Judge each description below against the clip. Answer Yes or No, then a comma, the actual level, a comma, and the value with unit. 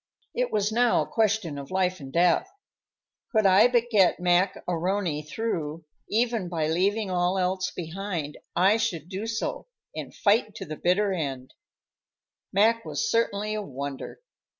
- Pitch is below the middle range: No, high, 190 Hz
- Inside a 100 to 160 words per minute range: Yes, average, 150 wpm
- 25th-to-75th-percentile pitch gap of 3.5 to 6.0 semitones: Yes, average, 4.4 semitones